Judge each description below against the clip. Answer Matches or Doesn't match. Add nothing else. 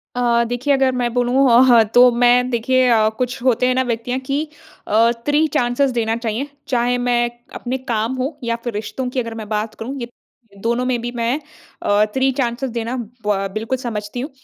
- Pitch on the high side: Matches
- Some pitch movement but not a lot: Doesn't match